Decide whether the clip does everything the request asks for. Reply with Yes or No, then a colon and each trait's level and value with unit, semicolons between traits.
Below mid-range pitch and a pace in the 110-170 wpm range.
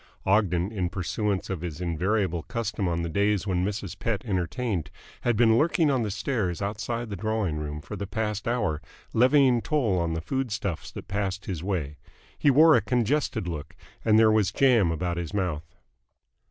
No: low, 100 Hz; average, 180 wpm